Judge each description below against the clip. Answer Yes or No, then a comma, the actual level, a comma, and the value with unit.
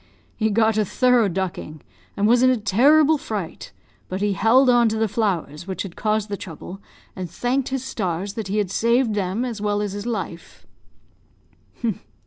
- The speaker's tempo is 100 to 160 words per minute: No, average, 180 wpm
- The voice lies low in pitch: No, high, 210 Hz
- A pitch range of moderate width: Yes, average, 3.7 semitones